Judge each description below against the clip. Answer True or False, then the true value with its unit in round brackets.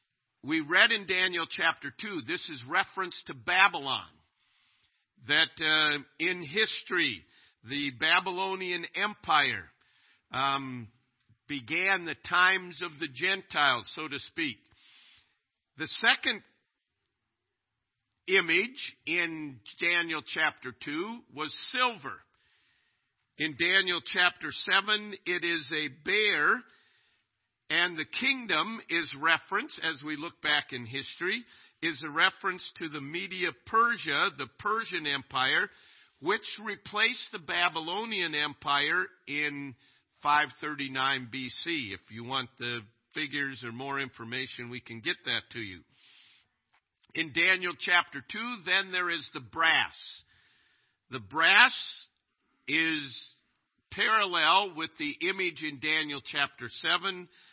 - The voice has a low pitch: False (160 Hz)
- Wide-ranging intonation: False (5.0 semitones)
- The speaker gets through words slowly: True (115 wpm)